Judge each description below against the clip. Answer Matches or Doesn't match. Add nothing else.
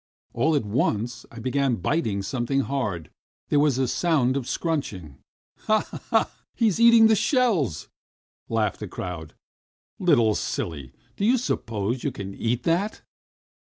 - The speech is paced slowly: Doesn't match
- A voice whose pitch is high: Doesn't match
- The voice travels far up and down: Matches